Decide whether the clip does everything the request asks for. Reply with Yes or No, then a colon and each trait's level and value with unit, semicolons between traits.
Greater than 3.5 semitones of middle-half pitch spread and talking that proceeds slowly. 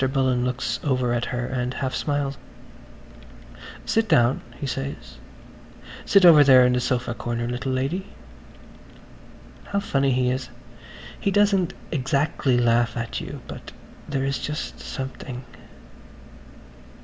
No: average, 2.7 semitones; slow, 125 wpm